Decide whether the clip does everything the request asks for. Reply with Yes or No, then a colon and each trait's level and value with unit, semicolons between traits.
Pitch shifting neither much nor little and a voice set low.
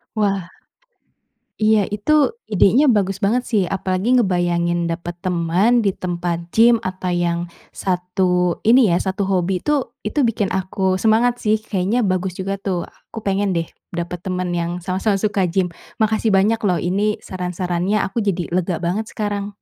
No: average, 3.0 semitones; high, 190 Hz